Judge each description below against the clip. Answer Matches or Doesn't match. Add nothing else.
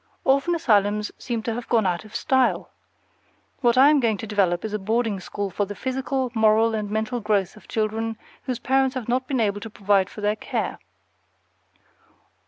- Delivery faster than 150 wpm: Matches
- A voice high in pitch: Matches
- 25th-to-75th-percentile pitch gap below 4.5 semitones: Matches